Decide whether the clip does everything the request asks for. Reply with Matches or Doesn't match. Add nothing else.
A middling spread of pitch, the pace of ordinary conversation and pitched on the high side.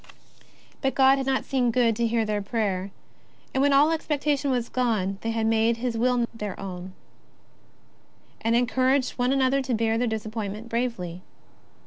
Matches